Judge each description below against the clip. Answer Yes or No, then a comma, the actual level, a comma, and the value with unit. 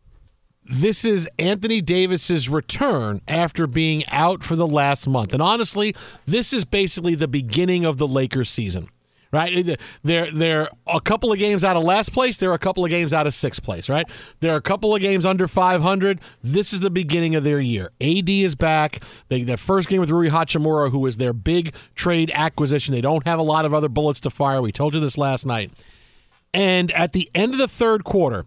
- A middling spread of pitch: Yes, average, 4.6 semitones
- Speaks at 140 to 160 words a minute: No, fast, 205 wpm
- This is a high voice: No, medium, 165 Hz